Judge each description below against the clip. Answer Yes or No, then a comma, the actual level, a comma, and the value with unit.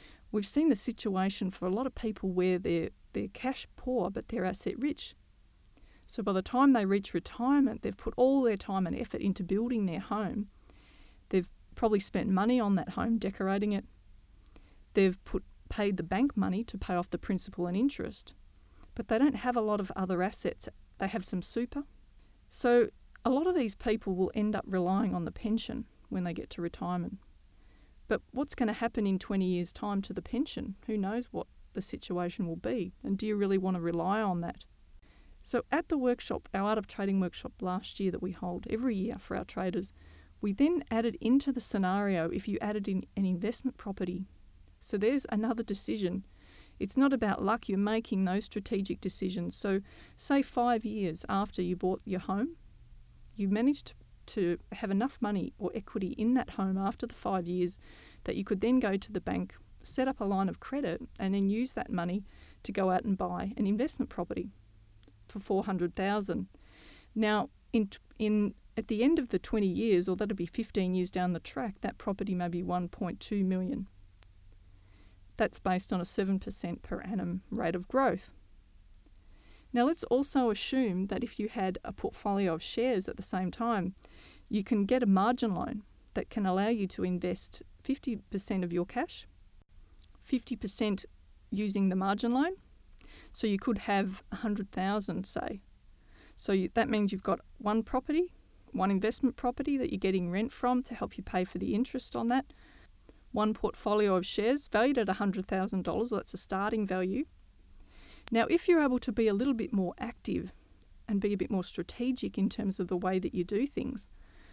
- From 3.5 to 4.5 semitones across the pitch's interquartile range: Yes, average, 4.0 semitones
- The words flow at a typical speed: Yes, average, 185 wpm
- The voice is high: Yes, high, 205 Hz